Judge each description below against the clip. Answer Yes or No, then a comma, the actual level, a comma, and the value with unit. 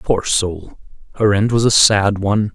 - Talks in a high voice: No, low, 100 Hz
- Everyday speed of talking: Yes, average, 190 wpm